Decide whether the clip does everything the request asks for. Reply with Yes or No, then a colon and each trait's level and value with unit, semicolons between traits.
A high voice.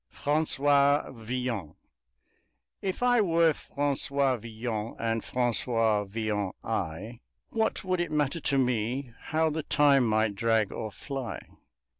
No: low, 125 Hz